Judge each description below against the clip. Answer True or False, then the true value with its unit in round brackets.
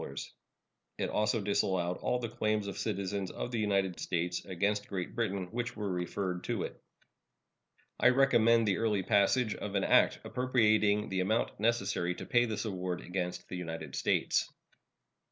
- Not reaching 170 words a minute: True (155 wpm)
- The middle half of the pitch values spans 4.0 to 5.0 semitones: False (3.1 semitones)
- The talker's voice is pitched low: True (100 Hz)